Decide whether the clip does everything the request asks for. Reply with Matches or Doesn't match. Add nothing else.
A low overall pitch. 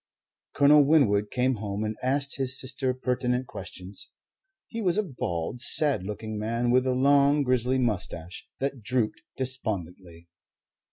Matches